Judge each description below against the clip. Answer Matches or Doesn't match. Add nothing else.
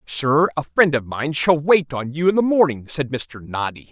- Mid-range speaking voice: Matches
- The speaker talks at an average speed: Doesn't match